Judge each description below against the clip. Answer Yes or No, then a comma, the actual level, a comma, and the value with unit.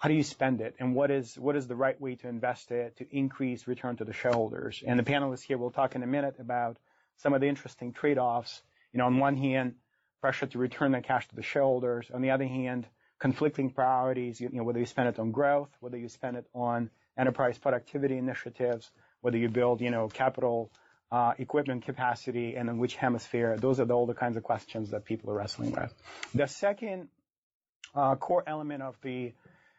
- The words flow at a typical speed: No, fast, 210 wpm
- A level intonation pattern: Yes, narrow, 2.1 semitones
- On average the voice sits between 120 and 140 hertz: Yes, low, 125 Hz